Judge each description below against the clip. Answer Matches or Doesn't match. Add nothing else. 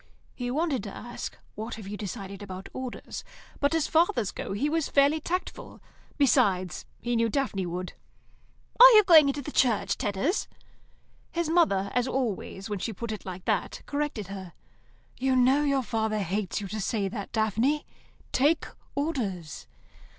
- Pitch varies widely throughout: Matches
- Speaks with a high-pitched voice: Matches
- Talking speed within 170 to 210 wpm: Doesn't match